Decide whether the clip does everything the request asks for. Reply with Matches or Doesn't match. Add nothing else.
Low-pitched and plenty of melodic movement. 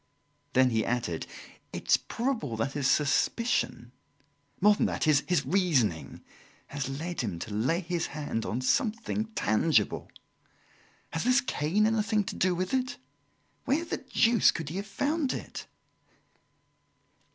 Doesn't match